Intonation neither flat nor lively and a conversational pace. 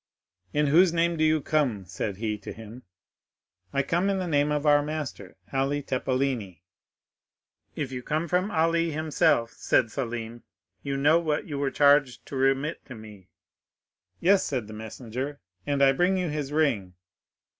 Yes: average, 4.8 semitones; average, 155 wpm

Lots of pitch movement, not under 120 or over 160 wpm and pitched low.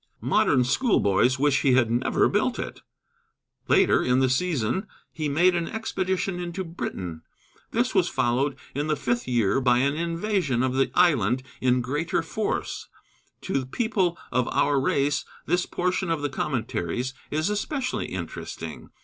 No: wide, 5.8 semitones; average, 150 wpm; medium, 145 Hz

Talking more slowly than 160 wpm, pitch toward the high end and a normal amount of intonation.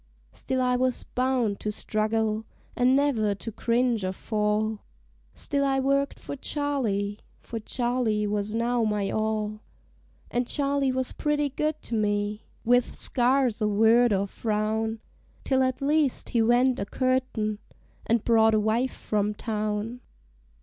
Yes: average, 145 wpm; high, 230 Hz; average, 3.3 semitones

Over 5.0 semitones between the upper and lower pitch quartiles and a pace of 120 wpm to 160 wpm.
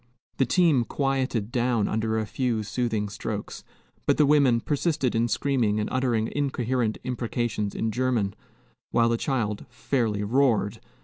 No: average, 3.1 semitones; average, 140 wpm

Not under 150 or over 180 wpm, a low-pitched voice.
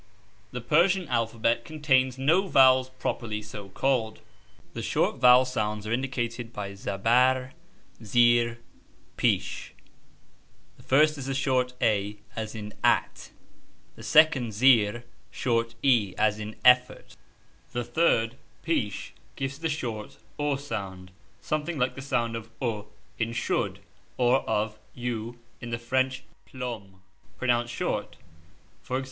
No: slow, 135 wpm; low, 120 Hz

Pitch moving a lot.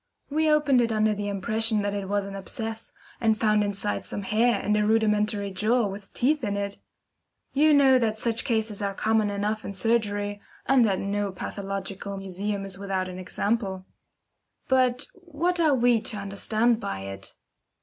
No: average, 2.8 semitones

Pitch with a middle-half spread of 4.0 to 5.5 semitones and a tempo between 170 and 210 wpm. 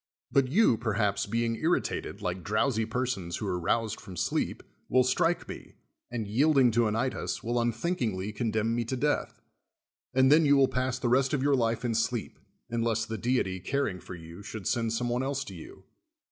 No: average, 3.2 semitones; average, 190 wpm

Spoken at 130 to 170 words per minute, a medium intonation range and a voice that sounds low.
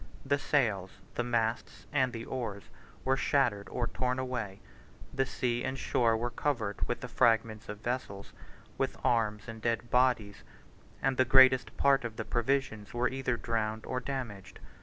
Yes: average, 165 wpm; average, 3.0 semitones; low, 120 Hz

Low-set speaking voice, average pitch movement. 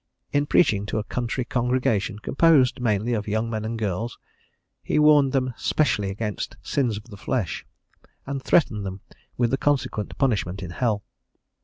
Yes: low, 115 Hz; average, 4.1 semitones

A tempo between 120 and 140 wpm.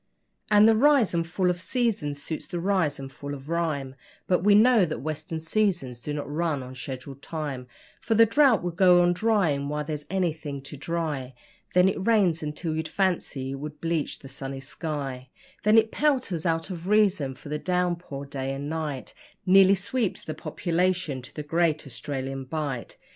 No: average, 185 wpm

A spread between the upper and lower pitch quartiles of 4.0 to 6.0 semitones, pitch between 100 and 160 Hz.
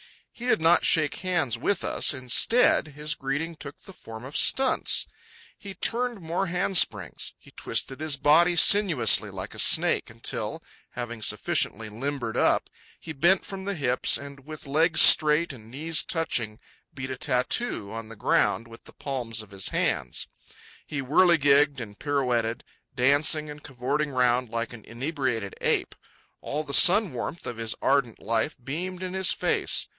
Yes: wide, 5.5 semitones; medium, 140 Hz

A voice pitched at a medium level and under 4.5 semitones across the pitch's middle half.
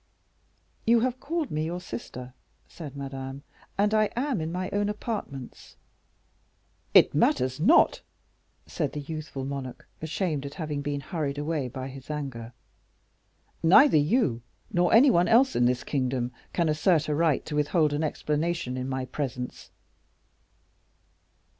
No: medium, 150 Hz; average, 5.0 semitones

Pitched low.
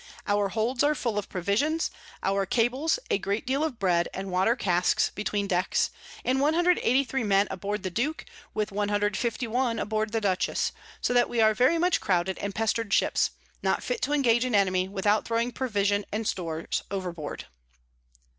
No: high, 215 Hz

